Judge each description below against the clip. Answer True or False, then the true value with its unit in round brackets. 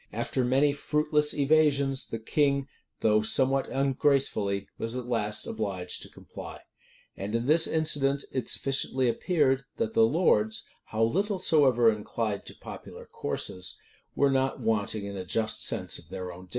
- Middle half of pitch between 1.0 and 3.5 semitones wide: False (4.8 semitones)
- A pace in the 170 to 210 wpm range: False (155 wpm)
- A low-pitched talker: True (130 Hz)